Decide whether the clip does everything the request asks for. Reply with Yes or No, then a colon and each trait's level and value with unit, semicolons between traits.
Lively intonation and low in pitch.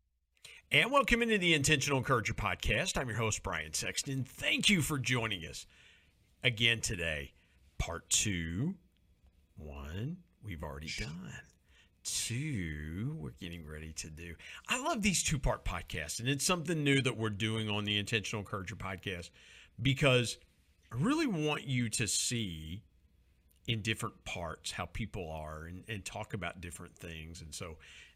Yes: wide, 7.5 semitones; low, 100 Hz